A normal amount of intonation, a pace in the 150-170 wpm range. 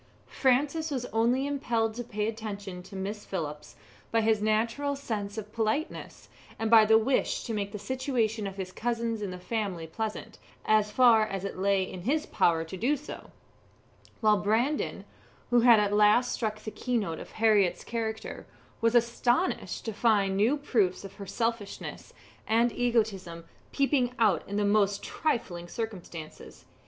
Yes: average, 3.1 semitones; average, 165 wpm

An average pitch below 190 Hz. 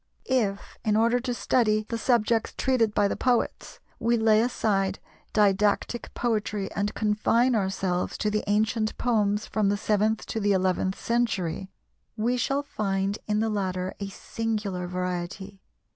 No: high, 210 Hz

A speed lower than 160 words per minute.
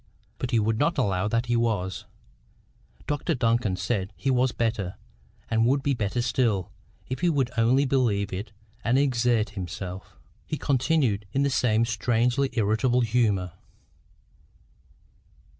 Yes: average, 140 wpm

